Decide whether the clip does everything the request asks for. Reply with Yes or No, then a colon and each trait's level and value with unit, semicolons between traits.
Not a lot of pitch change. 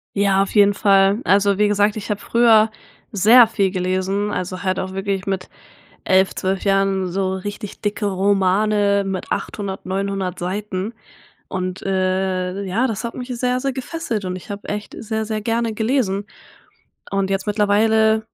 Yes: narrow, 2.2 semitones